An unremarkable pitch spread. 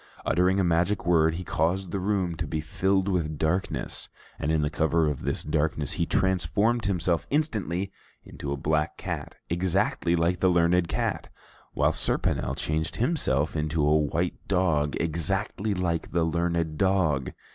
Yes: average, 3.3 semitones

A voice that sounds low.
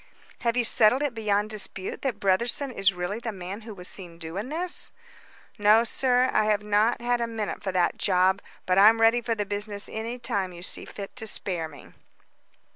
No: high, 210 Hz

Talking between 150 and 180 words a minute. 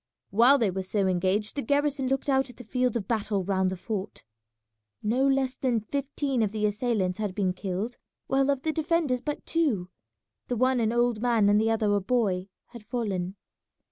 No: average, 195 wpm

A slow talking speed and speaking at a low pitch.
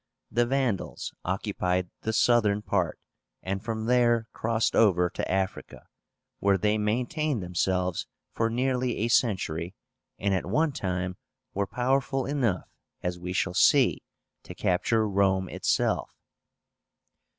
Yes: slow, 125 wpm; low, 105 Hz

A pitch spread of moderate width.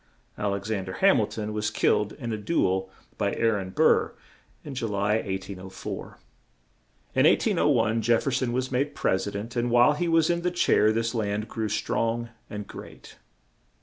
Yes: average, 3.2 semitones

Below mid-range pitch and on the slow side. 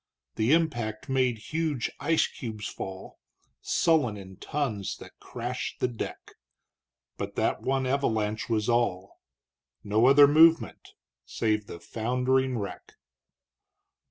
Yes: low, 120 Hz; slow, 115 wpm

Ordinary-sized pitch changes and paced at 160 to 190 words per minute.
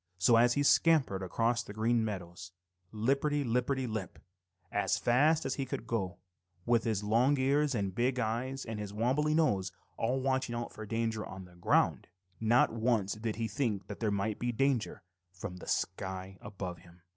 Yes: average, 4.3 semitones; average, 180 wpm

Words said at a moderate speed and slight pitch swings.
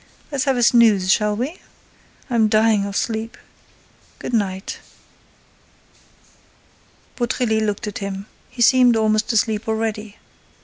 No: slow, 105 wpm; narrow, 2.1 semitones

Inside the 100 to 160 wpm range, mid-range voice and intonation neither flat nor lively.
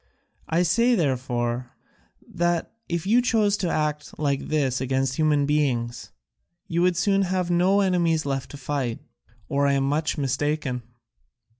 Yes: average, 145 wpm; medium, 150 Hz; average, 4.5 semitones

